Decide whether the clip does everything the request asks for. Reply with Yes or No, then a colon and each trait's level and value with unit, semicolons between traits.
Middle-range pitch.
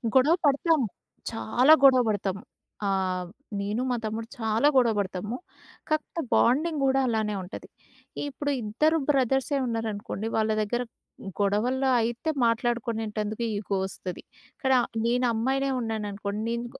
No: high, 230 Hz